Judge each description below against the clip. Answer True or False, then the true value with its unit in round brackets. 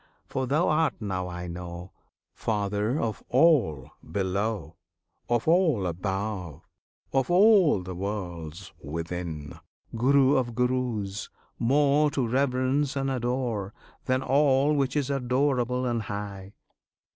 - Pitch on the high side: False (120 Hz)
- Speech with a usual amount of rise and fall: False (6.0 semitones)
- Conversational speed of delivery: False (115 wpm)